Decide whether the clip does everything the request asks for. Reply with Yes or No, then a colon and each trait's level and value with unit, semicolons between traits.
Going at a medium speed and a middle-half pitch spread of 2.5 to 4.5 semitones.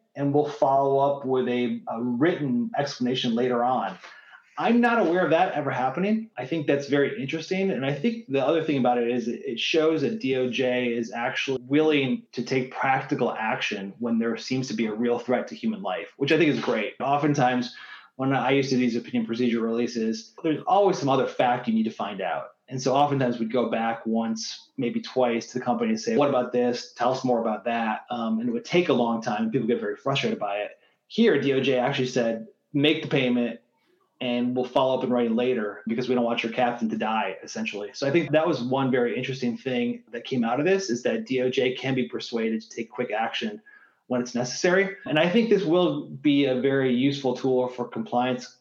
No: fast, 220 wpm; average, 3.4 semitones